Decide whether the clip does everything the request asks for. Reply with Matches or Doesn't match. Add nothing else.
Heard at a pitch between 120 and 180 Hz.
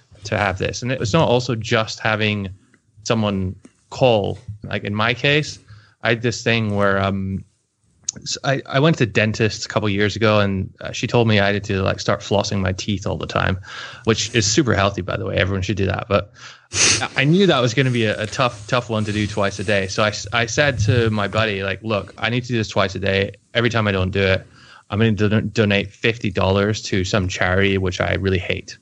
Doesn't match